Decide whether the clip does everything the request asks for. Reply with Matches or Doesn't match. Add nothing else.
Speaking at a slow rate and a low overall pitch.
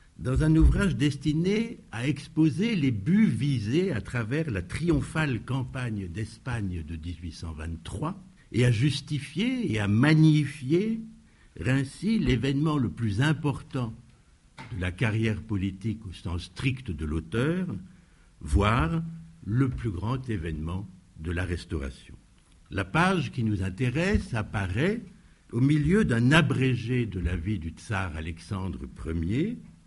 Matches